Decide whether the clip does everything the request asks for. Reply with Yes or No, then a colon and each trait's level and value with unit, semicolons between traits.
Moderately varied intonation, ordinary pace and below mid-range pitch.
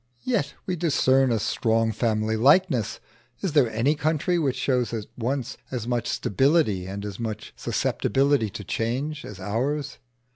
Yes: average, 4.8 semitones; average, 150 wpm; low, 125 Hz